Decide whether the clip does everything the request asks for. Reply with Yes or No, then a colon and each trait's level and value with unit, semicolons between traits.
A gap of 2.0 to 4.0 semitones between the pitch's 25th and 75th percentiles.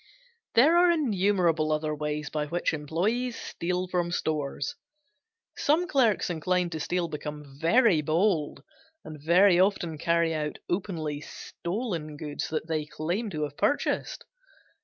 No: average, 4.5 semitones